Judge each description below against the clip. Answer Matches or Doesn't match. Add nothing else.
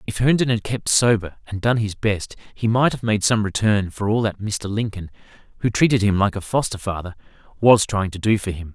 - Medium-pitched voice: Doesn't match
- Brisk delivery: Matches